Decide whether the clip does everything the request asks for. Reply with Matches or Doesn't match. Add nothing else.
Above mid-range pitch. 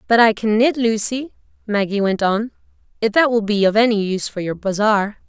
Matches